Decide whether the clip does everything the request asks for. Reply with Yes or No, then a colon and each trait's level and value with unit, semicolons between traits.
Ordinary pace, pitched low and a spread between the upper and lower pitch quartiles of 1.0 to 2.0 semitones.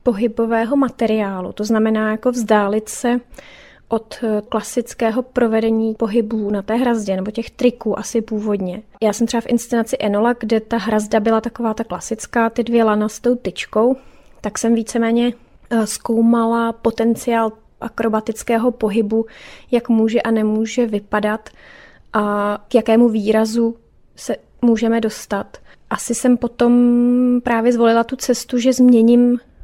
No: average, 135 wpm; high, 230 Hz; narrow, 1.6 semitones